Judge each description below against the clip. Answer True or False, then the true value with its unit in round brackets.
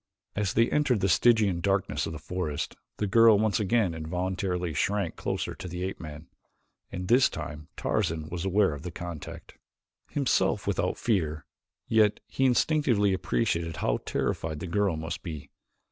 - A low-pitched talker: True (90 Hz)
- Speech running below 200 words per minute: True (160 wpm)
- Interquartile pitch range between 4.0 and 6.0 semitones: True (4.4 semitones)